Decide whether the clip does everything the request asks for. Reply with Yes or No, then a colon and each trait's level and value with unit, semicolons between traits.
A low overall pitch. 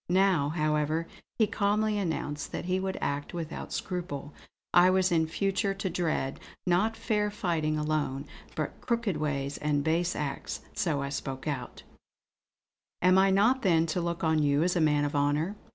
No: medium, 165 Hz